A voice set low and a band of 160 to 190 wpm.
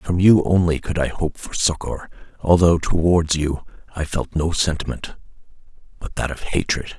Yes: very low, 80 Hz; average, 165 wpm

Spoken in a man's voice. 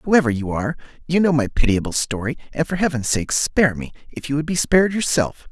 Yes: male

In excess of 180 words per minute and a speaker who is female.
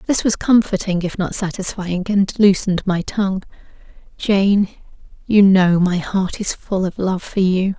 No: average, 160 wpm; female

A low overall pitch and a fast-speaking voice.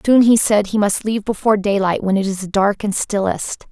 No: high, 205 Hz; fast, 225 wpm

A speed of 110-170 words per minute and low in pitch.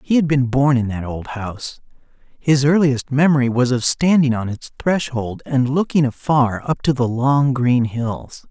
No: average, 185 wpm; low, 130 Hz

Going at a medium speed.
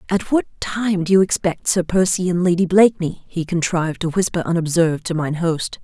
Yes: average, 195 wpm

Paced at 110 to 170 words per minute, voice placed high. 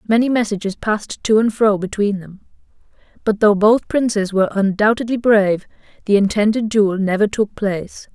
Yes: average, 155 wpm; high, 210 Hz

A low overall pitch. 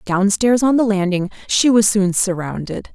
No: high, 205 Hz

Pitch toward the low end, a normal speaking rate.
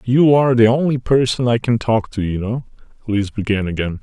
No: low, 115 Hz; fast, 210 wpm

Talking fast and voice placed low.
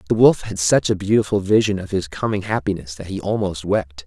Yes: fast, 220 wpm; very low, 95 Hz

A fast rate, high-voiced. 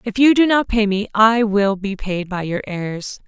Yes: fast, 240 wpm; high, 210 Hz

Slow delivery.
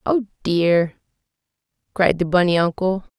Yes: slow, 115 wpm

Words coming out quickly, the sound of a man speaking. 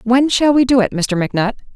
No: fast, 240 wpm; female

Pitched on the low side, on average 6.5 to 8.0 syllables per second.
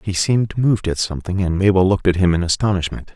Yes: very low, 95 Hz; 6.9 syllables/s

